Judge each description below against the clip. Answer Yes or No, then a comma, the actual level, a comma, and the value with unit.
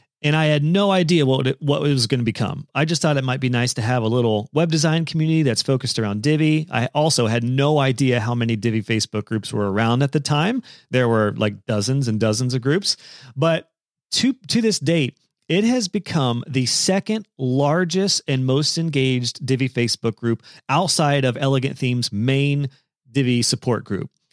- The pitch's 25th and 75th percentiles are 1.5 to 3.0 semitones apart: No, average, 4.6 semitones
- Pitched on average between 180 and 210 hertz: No, low, 135 Hz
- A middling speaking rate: Yes, average, 190 wpm